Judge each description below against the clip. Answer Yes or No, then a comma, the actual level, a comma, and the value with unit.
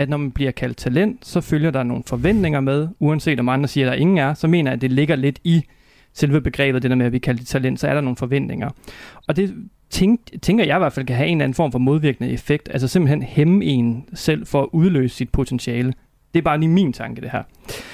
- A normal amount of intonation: Yes, average, 4.2 semitones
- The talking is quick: Yes, fast, 260 wpm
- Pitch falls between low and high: Yes, medium, 145 Hz